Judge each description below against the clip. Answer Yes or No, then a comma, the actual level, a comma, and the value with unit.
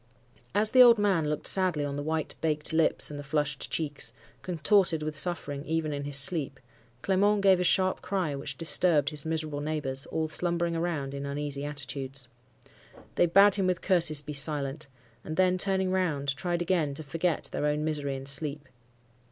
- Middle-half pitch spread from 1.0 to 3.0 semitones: No, average, 3.6 semitones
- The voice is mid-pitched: Yes, medium, 155 Hz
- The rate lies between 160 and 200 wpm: Yes, average, 180 wpm